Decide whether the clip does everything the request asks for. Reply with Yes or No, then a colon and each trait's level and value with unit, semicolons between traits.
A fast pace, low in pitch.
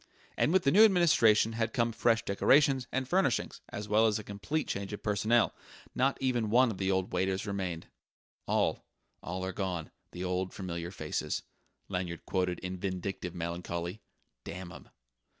No: average, 165 wpm; low, 100 Hz